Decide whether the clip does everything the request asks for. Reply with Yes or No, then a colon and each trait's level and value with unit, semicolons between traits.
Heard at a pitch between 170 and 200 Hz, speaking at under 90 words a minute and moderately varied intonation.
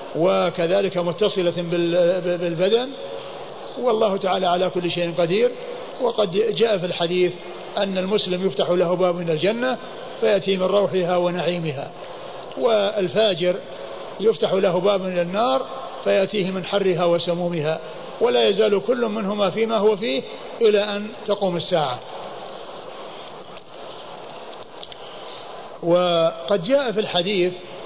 No: high, 190 Hz; average, 105 wpm; average, 3.6 semitones